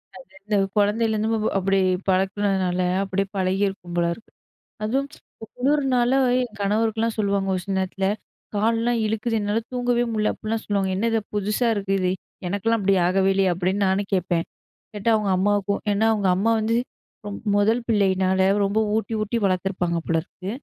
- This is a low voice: No, high, 205 Hz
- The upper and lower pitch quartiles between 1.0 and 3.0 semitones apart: Yes, average, 2.7 semitones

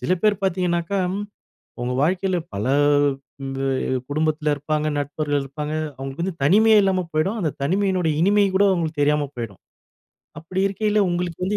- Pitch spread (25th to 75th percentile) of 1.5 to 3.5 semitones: No, average, 4.5 semitones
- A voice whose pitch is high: No, medium, 165 Hz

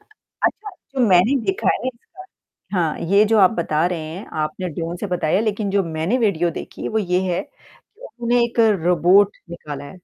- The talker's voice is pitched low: No, medium, 185 Hz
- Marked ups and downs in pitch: No, average, 5.0 semitones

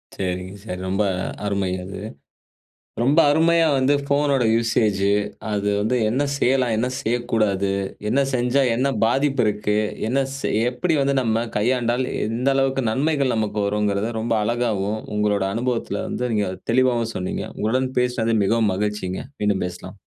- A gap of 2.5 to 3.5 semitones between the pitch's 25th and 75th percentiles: No, average, 3.9 semitones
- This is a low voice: Yes, low, 115 Hz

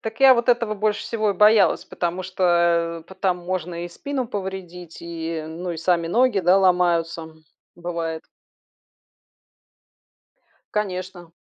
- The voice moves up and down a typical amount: Yes, average, 3.3 semitones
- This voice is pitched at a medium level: Yes, medium, 180 Hz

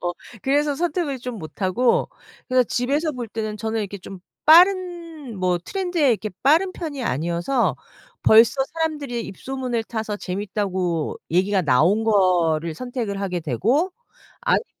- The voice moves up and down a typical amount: No, wide, 7.3 semitones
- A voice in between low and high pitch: No, high, 225 Hz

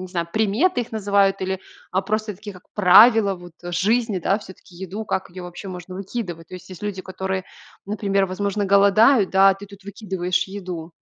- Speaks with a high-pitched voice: Yes, high, 195 Hz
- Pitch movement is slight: Yes, narrow, 2.1 semitones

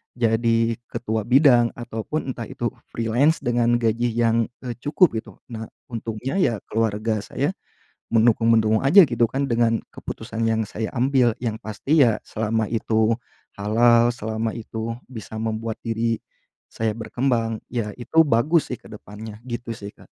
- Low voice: Yes, low, 115 Hz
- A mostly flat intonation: Yes, narrow, 1.5 semitones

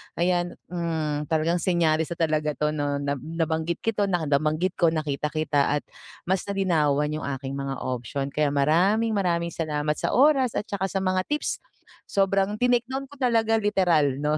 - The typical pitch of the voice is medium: Yes, medium, 165 Hz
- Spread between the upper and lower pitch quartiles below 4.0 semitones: No, average, 4.5 semitones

